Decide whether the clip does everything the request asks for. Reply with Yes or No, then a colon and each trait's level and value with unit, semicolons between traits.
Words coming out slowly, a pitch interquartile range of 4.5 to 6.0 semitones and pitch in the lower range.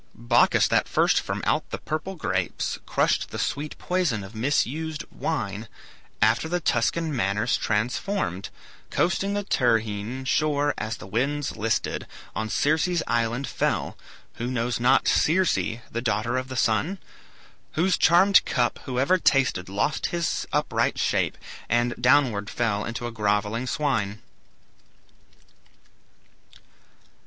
Yes: slow, 125 wpm; wide, 5.6 semitones; low, 125 Hz